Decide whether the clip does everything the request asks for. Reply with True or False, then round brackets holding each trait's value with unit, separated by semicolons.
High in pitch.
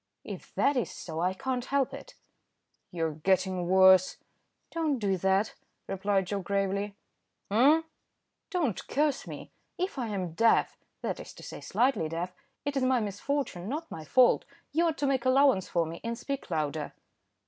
True (205 Hz)